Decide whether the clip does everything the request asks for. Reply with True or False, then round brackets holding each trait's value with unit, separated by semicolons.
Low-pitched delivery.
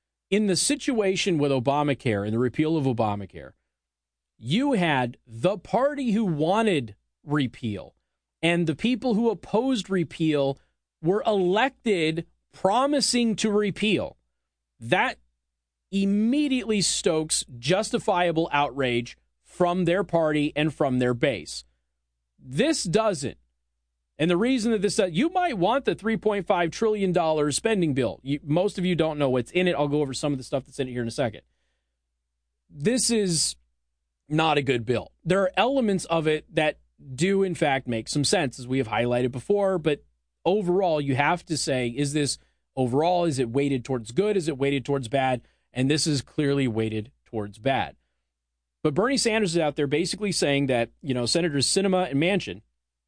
False (150 Hz)